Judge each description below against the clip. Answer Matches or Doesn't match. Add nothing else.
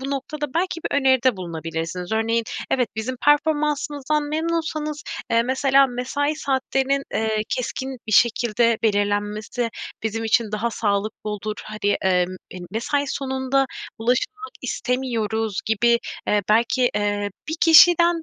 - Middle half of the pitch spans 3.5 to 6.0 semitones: Matches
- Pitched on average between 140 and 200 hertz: Doesn't match